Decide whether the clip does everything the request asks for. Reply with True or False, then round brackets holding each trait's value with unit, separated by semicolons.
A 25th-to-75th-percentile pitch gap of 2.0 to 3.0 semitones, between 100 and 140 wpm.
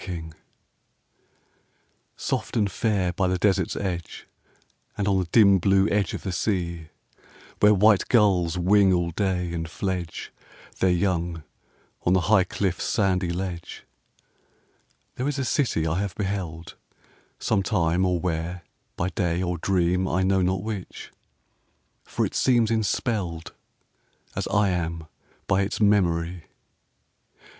True (2.6 semitones; 135 wpm)